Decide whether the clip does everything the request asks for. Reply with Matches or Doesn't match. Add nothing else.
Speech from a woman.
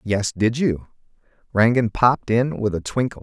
Doesn't match